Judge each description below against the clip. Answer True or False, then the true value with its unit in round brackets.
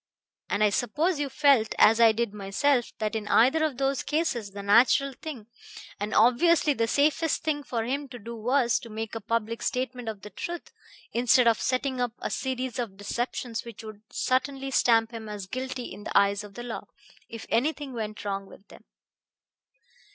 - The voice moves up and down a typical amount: True (3.7 semitones)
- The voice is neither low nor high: False (235 Hz)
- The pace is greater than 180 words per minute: True (190 wpm)